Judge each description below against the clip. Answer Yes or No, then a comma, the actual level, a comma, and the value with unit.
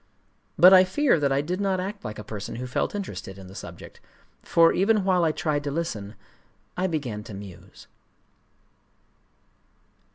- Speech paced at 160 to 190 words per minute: Yes, average, 165 wpm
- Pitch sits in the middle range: Yes, medium, 155 Hz